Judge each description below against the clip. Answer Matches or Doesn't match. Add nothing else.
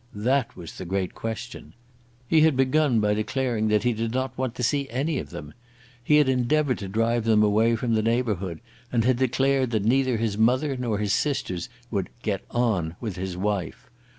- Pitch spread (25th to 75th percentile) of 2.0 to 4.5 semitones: Matches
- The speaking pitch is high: Doesn't match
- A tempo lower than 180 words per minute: Doesn't match